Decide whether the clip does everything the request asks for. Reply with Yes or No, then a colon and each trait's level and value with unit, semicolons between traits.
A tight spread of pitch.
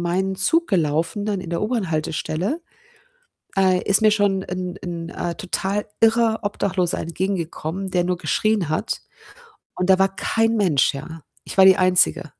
No: average, 3.0 semitones